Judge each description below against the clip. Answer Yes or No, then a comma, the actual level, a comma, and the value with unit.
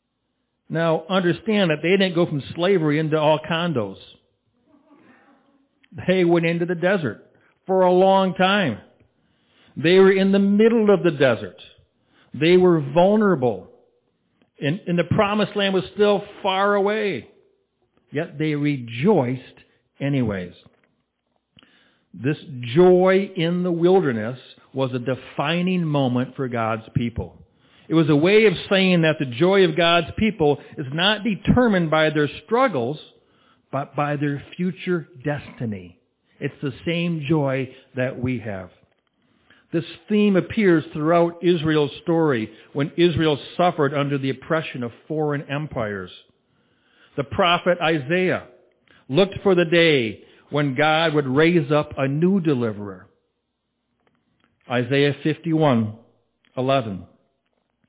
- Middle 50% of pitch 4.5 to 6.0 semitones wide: Yes, average, 5.2 semitones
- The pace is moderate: No, slow, 120 wpm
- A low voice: No, medium, 160 Hz